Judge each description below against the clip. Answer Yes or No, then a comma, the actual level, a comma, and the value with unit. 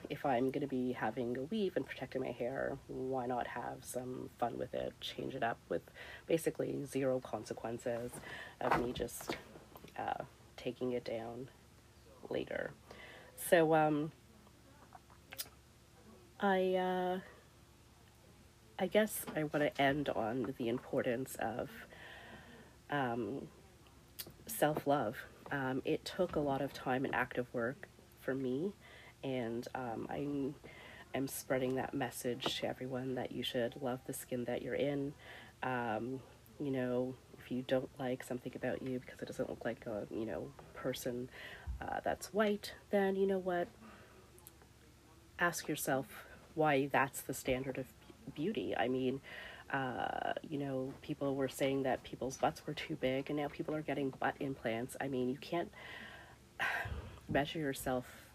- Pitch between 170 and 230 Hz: No, low, 130 Hz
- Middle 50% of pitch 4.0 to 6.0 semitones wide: No, average, 2.8 semitones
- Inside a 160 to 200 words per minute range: No, average, 145 wpm